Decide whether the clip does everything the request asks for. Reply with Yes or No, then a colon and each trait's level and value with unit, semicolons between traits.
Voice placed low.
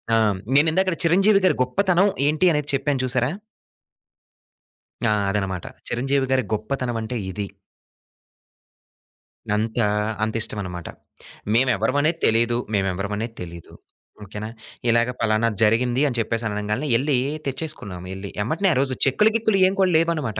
Yes: low, 125 Hz